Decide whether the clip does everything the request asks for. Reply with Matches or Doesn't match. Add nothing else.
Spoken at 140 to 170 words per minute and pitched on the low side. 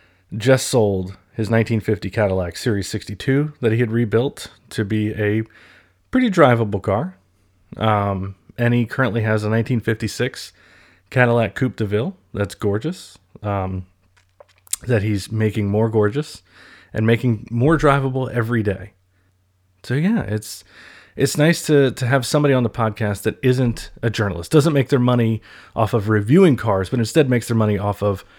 Matches